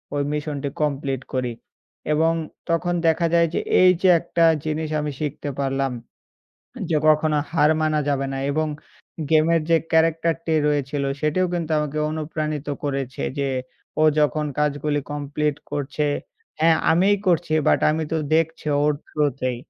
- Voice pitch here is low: No, medium, 150 Hz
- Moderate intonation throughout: No, narrow, 2.0 semitones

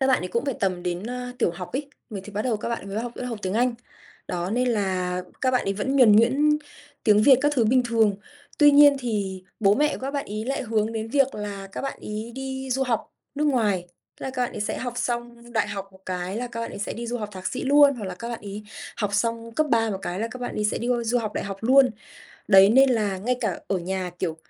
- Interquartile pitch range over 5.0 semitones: No, average, 4.1 semitones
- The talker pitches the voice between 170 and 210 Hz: No, high, 230 Hz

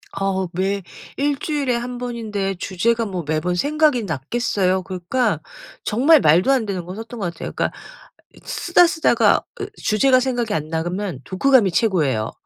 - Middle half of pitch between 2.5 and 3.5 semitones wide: No, wide, 5.6 semitones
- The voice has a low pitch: No, high, 205 Hz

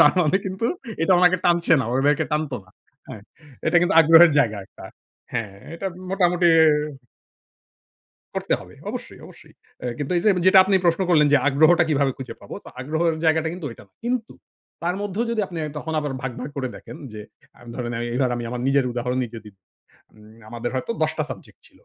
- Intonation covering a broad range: Yes, wide, 5.8 semitones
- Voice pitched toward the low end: No, medium, 150 Hz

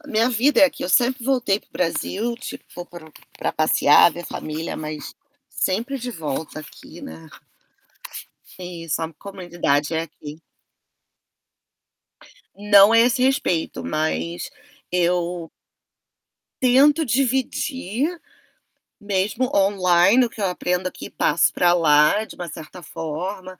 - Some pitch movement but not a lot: No, wide, 6.5 semitones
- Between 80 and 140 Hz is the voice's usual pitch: No, medium, 185 Hz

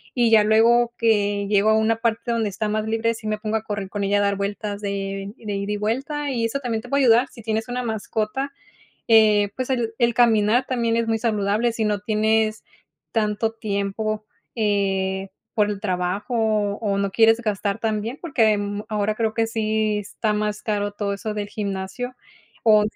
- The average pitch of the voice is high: Yes, high, 215 Hz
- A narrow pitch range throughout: Yes, narrow, 1.9 semitones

